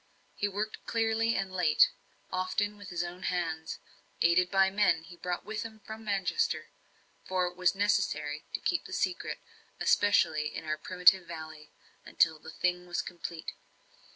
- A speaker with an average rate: Yes, average, 160 wpm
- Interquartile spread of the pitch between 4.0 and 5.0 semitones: No, average, 3.5 semitones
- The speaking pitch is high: No, medium, 180 Hz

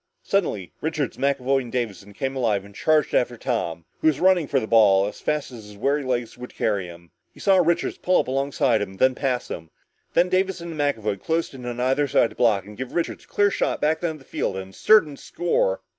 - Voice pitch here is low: Yes, low, 130 Hz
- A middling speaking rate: No, fast, 235 wpm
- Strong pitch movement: Yes, wide, 6.7 semitones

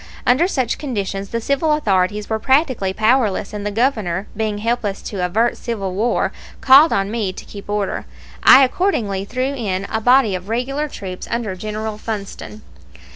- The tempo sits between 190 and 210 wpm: No, average, 165 wpm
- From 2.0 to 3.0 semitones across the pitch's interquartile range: No, average, 4.3 semitones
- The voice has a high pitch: Yes, high, 220 Hz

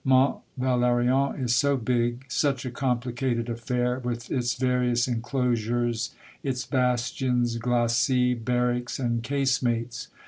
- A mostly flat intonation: Yes, narrow, 1.3 semitones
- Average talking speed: No, slow, 110 wpm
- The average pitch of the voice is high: No, low, 125 Hz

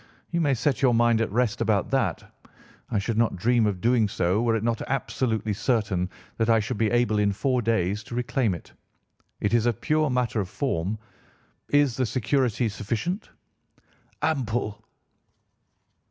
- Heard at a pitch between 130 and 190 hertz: No, low, 115 Hz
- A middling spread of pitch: Yes, average, 3.1 semitones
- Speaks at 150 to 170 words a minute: Yes, average, 165 wpm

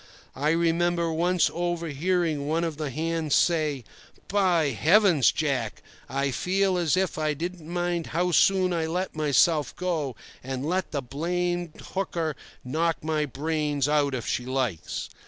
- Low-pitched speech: No, medium, 160 Hz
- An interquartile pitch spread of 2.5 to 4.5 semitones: Yes, average, 3.3 semitones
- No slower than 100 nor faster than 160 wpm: Yes, average, 150 wpm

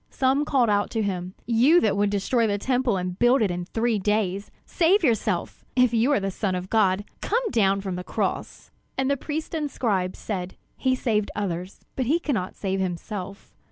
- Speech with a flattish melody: No, average, 5.2 semitones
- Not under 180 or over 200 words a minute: Yes, average, 195 wpm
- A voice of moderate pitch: No, high, 210 Hz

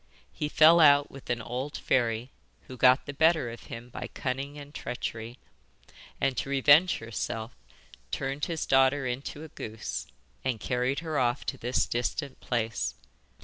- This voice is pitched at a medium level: No, low, 130 Hz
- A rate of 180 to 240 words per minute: No, average, 155 wpm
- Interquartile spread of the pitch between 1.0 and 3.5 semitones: Yes, average, 3.1 semitones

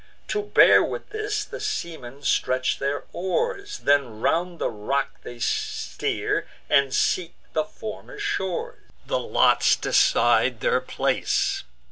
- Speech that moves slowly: Yes, slow, 125 wpm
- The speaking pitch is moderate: Yes, medium, 170 Hz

